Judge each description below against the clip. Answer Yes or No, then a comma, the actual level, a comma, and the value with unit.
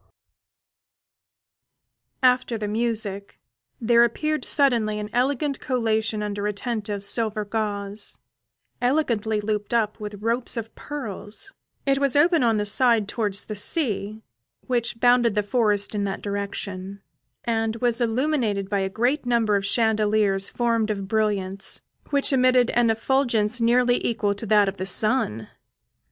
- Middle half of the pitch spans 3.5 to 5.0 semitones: No, average, 2.9 semitones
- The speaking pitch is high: Yes, high, 220 Hz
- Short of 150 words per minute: Yes, average, 140 wpm